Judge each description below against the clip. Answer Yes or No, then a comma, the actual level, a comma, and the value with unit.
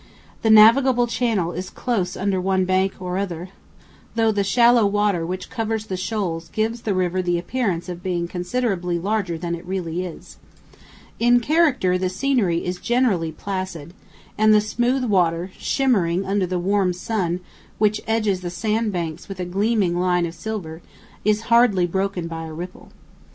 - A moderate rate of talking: Yes, average, 165 wpm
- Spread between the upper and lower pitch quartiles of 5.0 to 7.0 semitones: No, average, 3.7 semitones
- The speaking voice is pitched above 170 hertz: Yes, high, 190 Hz